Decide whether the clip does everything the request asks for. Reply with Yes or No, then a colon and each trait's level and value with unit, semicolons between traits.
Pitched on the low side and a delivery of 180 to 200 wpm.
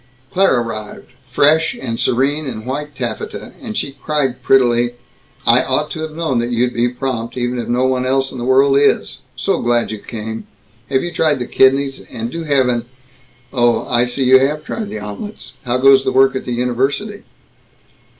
Yes: low, 130 Hz; average, 190 wpm